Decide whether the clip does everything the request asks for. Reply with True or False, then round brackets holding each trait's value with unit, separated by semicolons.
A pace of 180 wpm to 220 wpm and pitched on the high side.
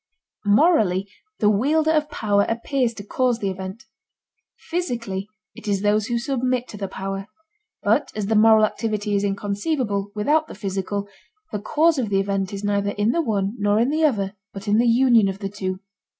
True (185 wpm; 210 Hz)